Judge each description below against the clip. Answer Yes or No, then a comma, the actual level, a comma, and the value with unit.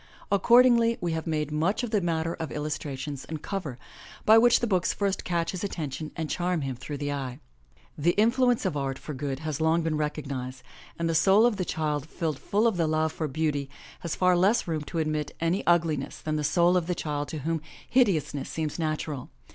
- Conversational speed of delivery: No, fast, 210 wpm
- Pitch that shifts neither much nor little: Yes, average, 3.5 semitones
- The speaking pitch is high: No, medium, 160 Hz